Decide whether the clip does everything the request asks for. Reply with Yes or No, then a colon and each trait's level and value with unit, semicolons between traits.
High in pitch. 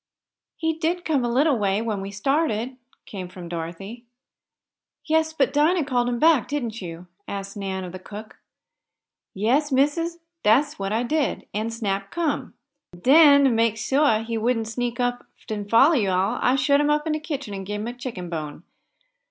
Yes: high, 235 Hz